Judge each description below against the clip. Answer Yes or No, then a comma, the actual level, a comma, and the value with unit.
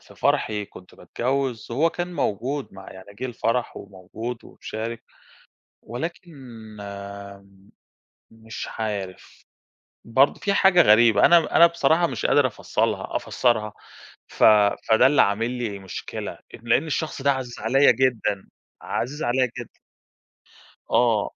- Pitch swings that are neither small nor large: Yes, average, 4.5 semitones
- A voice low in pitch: Yes, low, 120 Hz